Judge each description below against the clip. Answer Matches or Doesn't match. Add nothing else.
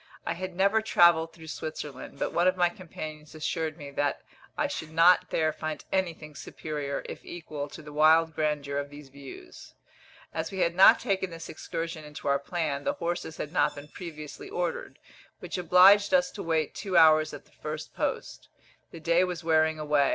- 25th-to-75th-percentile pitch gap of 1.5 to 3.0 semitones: Matches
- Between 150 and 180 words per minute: Doesn't match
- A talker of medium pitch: Matches